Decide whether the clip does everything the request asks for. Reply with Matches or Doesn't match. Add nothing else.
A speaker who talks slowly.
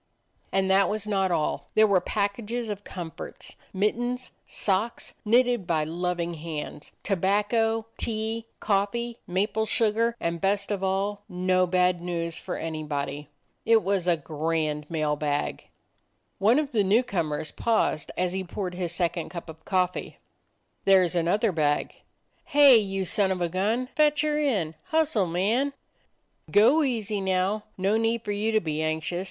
Doesn't match